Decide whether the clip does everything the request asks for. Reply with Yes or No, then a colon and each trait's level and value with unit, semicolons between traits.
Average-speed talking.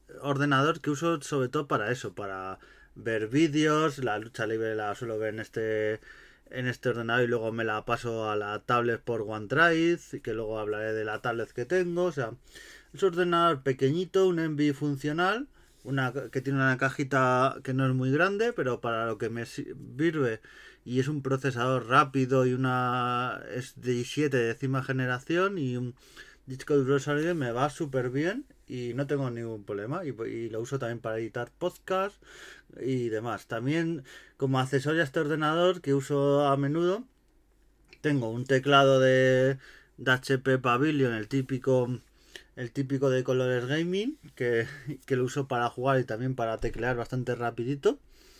Yes: average, 170 wpm